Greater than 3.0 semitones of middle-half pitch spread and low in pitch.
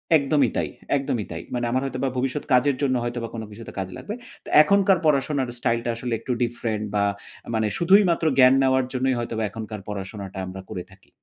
Yes: average, 3.7 semitones; low, 120 Hz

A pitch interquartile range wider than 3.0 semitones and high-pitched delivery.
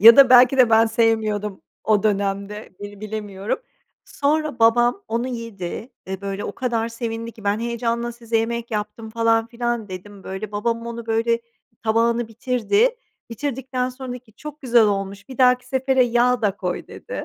No: average, 2.7 semitones; high, 230 Hz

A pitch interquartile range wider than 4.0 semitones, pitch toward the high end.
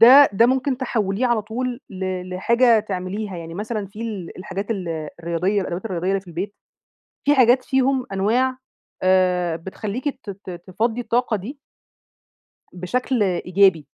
Yes: average, 4.7 semitones; high, 205 Hz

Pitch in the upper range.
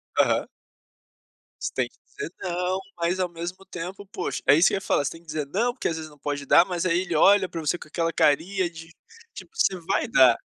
No: medium, 175 Hz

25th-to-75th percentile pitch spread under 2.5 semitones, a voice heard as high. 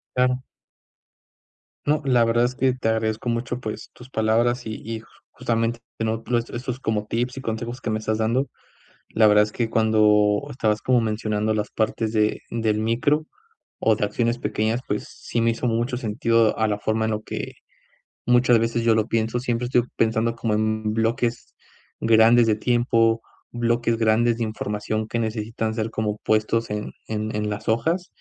No: narrow, 1.6 semitones; low, 115 Hz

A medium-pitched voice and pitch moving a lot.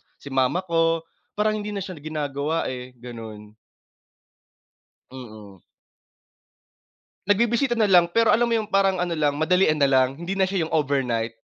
Yes: medium, 160 Hz; wide, 6.8 semitones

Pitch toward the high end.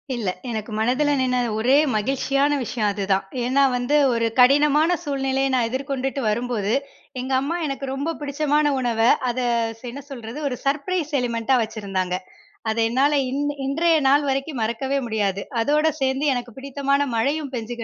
Yes: very high, 265 Hz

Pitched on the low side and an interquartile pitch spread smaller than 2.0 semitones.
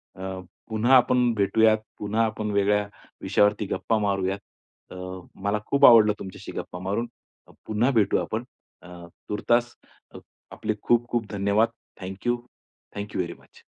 No: low, 105 Hz; narrow, 2.5 semitones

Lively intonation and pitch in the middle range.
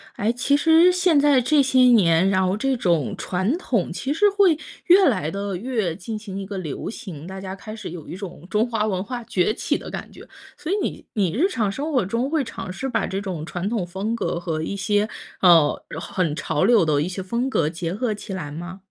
No: wide, 5.8 semitones; high, 205 Hz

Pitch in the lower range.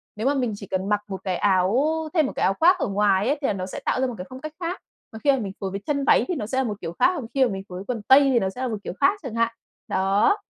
No: high, 225 Hz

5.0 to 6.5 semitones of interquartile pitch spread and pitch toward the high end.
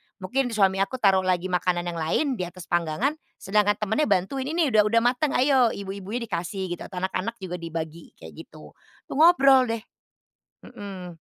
Yes: wide, 5.5 semitones; high, 195 Hz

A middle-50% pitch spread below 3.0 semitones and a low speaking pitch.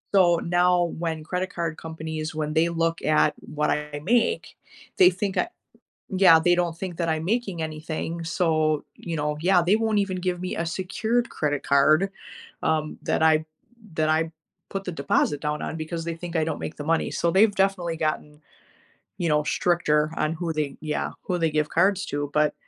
No: narrow, 2.6 semitones; medium, 165 Hz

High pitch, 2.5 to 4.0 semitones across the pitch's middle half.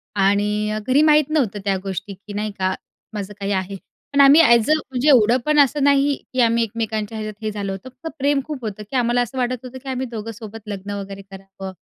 No: high, 225 Hz; average, 4.4 semitones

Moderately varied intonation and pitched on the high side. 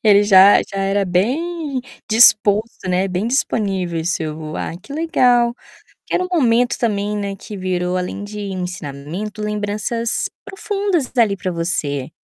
Yes: average, 4.5 semitones; high, 205 Hz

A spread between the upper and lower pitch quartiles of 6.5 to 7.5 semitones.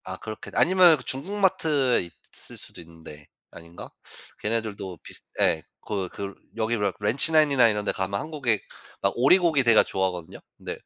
Yes: wide, 7.1 semitones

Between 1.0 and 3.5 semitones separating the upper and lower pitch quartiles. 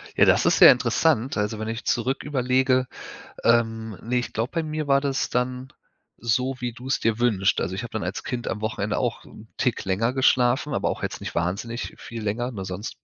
Yes: average, 2.8 semitones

